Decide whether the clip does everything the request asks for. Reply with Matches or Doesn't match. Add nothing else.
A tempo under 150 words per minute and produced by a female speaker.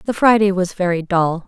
Doesn't match